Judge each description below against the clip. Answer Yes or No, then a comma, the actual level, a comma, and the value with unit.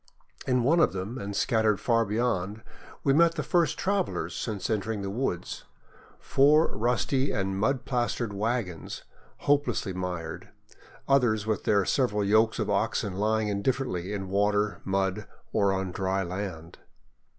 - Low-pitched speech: Yes, low, 105 Hz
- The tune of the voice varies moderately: Yes, average, 4.3 semitones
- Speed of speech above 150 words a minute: No, average, 145 wpm